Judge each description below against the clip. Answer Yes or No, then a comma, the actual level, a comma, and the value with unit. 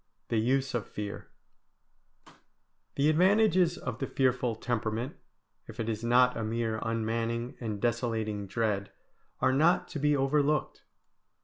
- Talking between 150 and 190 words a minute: No, slow, 135 wpm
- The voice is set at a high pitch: No, low, 120 Hz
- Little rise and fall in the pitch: No, average, 3.6 semitones